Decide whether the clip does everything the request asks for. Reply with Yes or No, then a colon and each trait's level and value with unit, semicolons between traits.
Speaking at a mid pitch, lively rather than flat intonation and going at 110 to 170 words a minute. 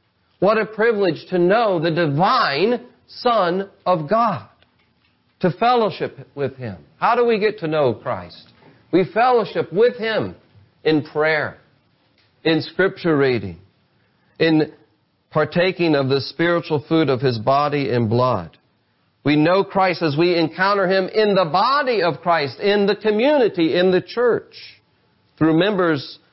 Yes: medium, 165 Hz; wide, 5.7 semitones; average, 140 wpm